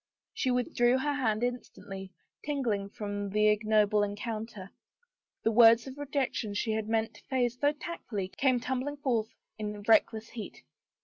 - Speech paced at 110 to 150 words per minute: Yes, average, 145 wpm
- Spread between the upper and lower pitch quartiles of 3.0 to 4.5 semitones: Yes, average, 3.3 semitones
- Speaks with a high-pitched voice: Yes, high, 225 Hz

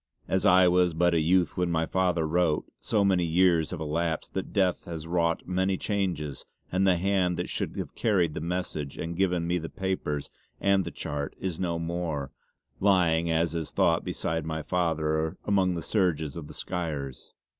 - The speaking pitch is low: Yes, very low, 85 Hz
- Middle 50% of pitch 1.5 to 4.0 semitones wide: Yes, narrow, 2.5 semitones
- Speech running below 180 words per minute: No, average, 185 wpm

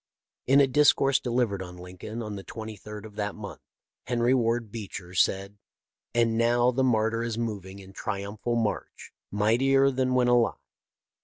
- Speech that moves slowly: No, average, 155 wpm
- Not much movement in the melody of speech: No, average, 3.1 semitones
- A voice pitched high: No, low, 115 Hz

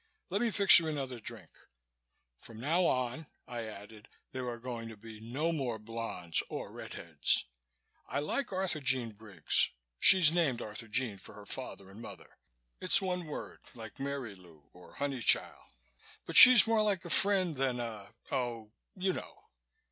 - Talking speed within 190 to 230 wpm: No, average, 155 wpm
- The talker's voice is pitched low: Yes, low, 125 Hz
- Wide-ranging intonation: Yes, wide, 6.6 semitones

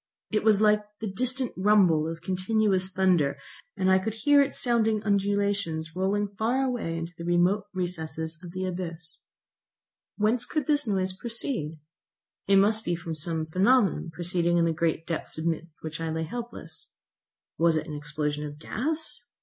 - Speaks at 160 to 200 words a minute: Yes, average, 165 wpm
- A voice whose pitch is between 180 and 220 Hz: Yes, medium, 185 Hz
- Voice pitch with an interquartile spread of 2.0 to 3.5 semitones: No, average, 4.7 semitones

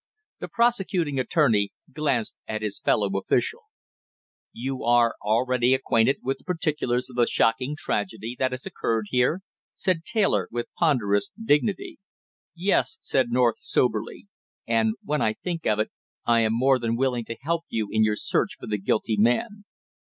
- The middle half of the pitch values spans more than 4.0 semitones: Yes, average, 5.2 semitones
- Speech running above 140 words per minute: Yes, average, 160 wpm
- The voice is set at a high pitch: No, low, 125 Hz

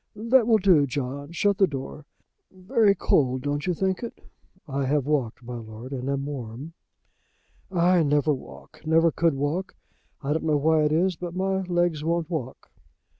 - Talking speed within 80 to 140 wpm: No, average, 175 wpm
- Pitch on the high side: No, medium, 155 Hz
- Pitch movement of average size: Yes, average, 4.6 semitones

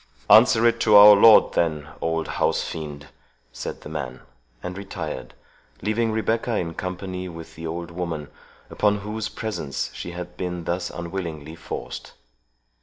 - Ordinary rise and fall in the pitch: Yes, average, 4.3 semitones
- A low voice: Yes, very low, 90 Hz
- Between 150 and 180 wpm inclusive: No, average, 140 wpm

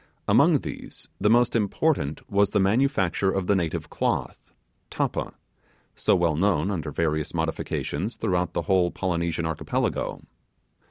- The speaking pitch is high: No, very low, 95 Hz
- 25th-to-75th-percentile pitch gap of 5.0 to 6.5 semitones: No, average, 3.8 semitones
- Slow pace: Yes, slow, 130 wpm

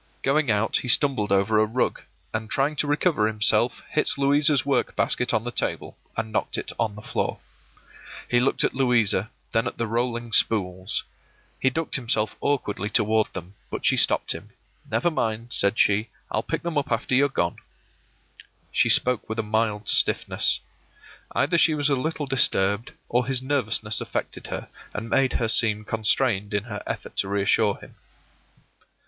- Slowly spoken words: No, average, 170 wpm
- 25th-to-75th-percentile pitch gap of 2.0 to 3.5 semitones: No, average, 4.1 semitones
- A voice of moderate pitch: No, low, 115 Hz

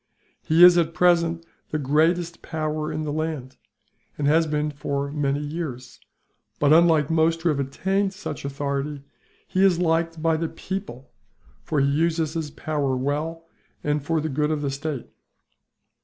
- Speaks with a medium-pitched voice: Yes, medium, 155 Hz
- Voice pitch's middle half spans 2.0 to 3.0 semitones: Yes, narrow, 2.4 semitones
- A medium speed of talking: Yes, average, 165 wpm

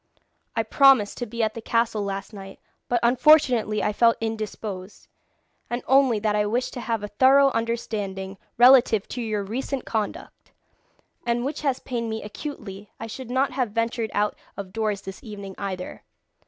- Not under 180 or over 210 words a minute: No, average, 170 wpm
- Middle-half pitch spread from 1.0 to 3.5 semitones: Yes, average, 3.0 semitones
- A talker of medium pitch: No, high, 225 Hz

